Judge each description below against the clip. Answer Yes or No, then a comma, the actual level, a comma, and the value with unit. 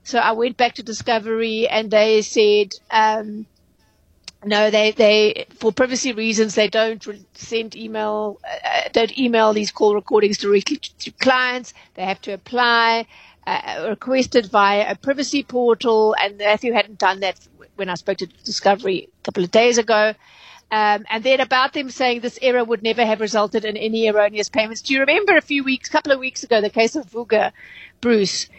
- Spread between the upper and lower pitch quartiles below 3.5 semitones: Yes, average, 2.7 semitones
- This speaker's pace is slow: No, average, 180 wpm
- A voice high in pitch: Yes, high, 220 Hz